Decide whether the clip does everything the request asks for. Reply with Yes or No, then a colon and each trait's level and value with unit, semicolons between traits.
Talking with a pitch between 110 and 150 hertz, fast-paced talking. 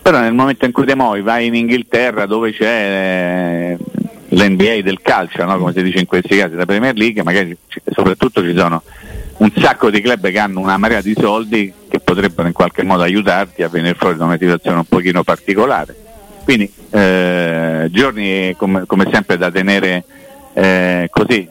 No: very low, 95 Hz; fast, 180 wpm